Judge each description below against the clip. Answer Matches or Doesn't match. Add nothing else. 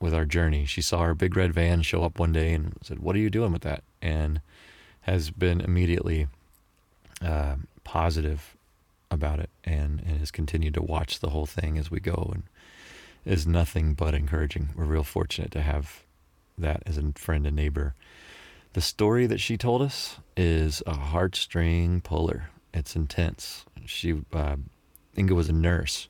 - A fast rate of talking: Doesn't match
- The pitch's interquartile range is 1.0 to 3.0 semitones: Matches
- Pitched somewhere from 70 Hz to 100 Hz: Matches